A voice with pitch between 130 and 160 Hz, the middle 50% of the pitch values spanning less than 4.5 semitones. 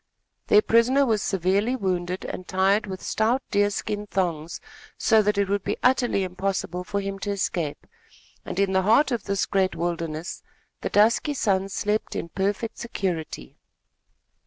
No: high, 195 Hz; narrow, 2.5 semitones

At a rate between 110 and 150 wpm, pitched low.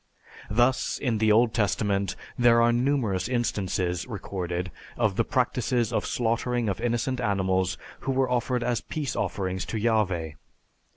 Yes: average, 140 wpm; low, 115 Hz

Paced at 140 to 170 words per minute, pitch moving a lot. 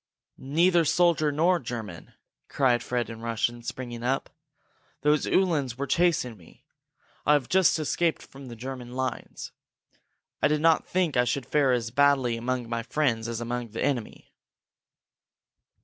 No: average, 150 wpm; average, 4.2 semitones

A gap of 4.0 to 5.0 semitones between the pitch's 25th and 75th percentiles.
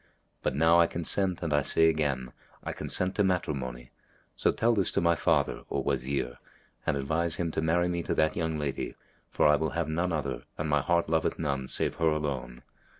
No: average, 3.3 semitones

